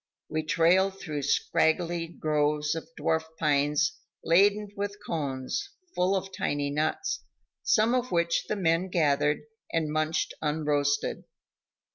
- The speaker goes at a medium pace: No, slow, 120 wpm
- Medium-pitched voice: Yes, medium, 160 Hz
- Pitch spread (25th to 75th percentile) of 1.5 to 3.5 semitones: No, average, 3.9 semitones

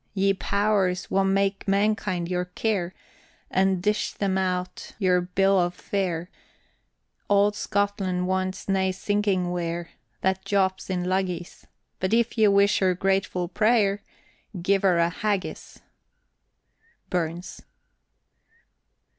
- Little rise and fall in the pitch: Yes, narrow, 1.7 semitones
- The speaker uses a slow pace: Yes, slow, 115 wpm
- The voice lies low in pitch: No, high, 190 Hz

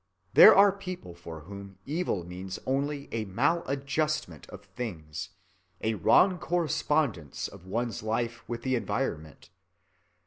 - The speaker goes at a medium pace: No, slow, 125 wpm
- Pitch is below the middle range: Yes, low, 120 Hz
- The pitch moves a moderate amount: No, wide, 8.1 semitones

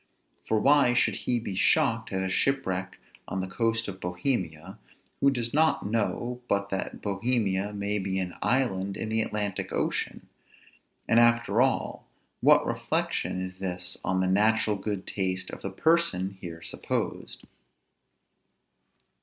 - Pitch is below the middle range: Yes, low, 100 Hz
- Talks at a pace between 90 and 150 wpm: Yes, average, 145 wpm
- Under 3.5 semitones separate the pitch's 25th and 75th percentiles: No, average, 3.8 semitones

